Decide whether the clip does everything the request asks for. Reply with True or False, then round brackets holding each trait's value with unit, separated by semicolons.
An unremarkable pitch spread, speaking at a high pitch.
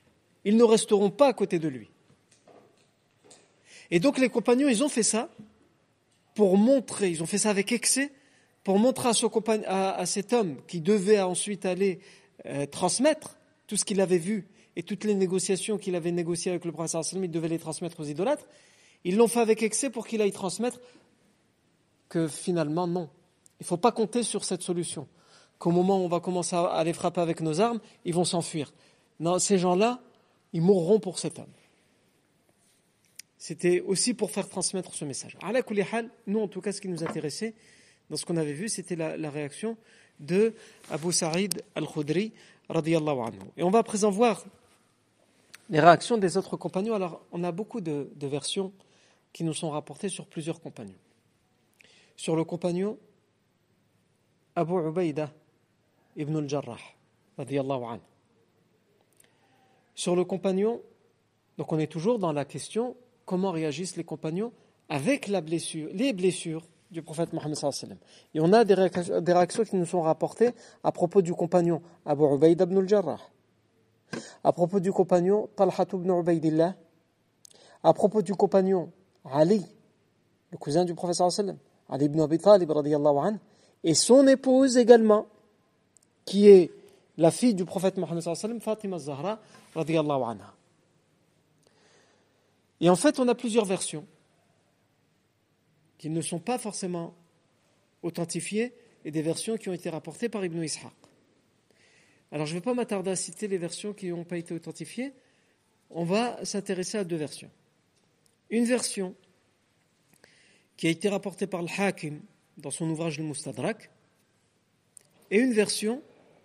False (4.5 semitones; 180 Hz)